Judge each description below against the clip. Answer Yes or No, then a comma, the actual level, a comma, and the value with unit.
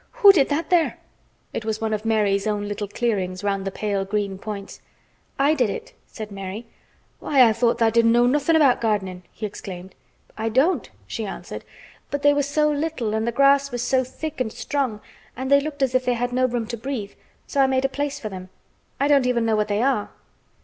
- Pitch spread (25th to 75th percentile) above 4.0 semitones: Yes, average, 4.8 semitones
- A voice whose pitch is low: No, high, 235 Hz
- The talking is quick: Yes, fast, 220 wpm